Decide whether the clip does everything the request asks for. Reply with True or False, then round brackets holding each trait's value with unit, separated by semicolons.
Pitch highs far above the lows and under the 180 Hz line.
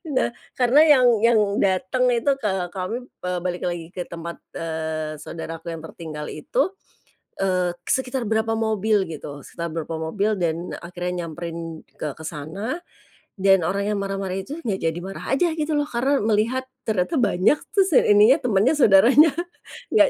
False (6.0 semitones; 195 Hz)